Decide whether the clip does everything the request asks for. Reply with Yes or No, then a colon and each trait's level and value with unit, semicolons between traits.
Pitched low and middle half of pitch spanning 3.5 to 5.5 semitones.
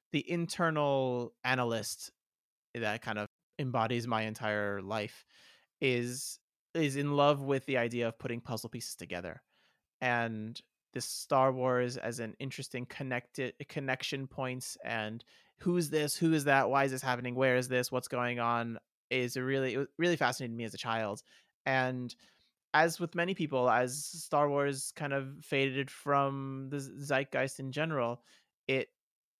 No: low, 130 Hz; average, 3.0 semitones